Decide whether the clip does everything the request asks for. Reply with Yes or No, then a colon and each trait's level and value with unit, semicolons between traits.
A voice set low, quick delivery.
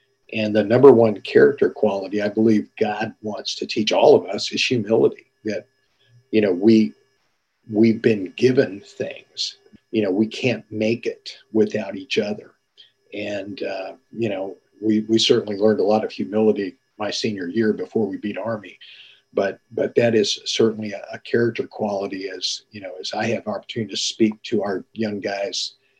No: low, 110 Hz; average, 175 wpm